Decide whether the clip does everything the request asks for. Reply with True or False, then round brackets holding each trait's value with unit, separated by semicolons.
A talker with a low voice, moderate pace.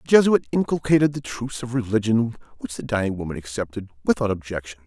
True (115 Hz; 175 wpm)